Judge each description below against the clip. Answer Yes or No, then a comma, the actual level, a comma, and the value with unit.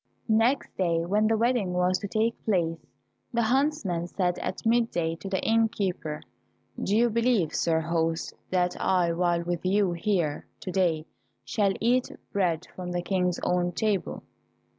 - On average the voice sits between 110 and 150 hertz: No, medium, 185 Hz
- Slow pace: No, average, 160 wpm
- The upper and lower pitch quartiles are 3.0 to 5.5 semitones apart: Yes, average, 4.0 semitones